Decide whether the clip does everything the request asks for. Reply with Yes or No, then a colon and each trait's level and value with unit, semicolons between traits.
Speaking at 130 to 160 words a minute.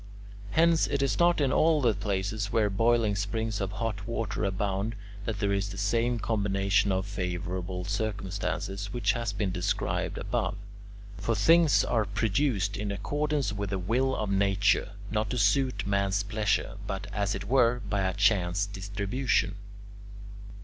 Yes: average, 155 wpm